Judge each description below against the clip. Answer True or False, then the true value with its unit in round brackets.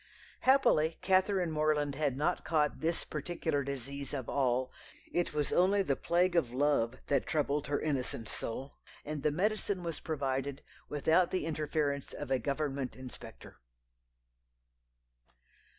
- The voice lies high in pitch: False (150 Hz)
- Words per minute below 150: True (135 wpm)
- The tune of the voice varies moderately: True (3.4 semitones)